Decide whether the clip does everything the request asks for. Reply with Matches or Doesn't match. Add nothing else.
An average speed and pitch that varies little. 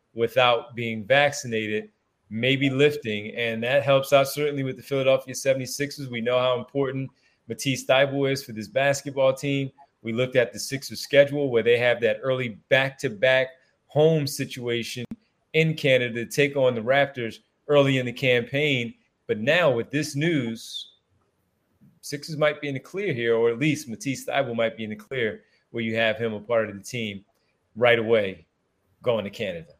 Doesn't match